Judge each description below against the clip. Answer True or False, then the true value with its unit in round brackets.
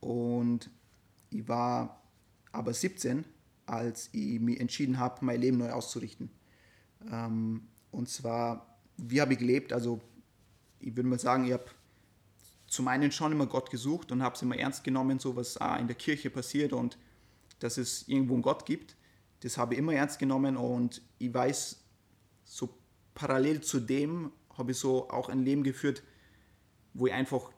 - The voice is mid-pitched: False (125 Hz)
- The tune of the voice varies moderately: False (2.2 semitones)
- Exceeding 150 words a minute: True (165 wpm)